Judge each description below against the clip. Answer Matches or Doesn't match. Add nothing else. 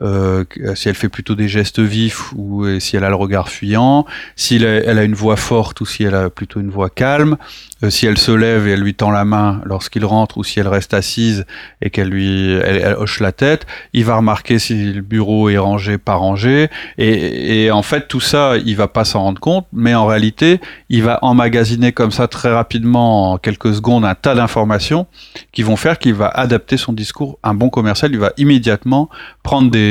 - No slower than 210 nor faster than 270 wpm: Matches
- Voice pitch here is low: Matches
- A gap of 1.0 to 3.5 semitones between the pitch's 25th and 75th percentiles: Matches